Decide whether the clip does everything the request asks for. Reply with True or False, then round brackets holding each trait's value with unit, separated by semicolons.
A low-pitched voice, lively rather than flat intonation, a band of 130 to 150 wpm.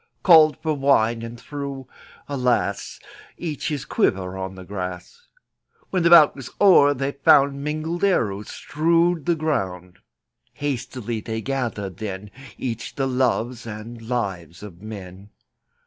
True (125 Hz; 6.2 semitones; 140 wpm)